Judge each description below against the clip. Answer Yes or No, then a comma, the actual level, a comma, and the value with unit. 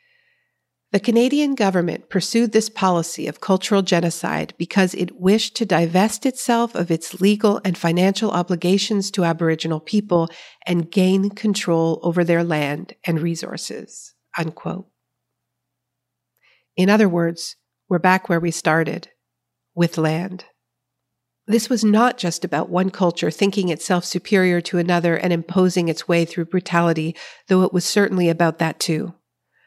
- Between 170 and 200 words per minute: No, average, 140 wpm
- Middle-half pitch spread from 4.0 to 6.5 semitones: No, average, 3.1 semitones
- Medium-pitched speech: Yes, medium, 180 Hz